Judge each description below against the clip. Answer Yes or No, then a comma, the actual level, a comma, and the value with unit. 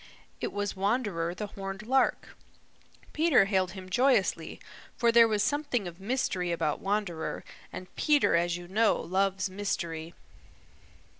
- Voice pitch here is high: Yes, high, 195 Hz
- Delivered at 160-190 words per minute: No, slow, 135 wpm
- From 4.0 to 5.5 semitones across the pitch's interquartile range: Yes, average, 4.3 semitones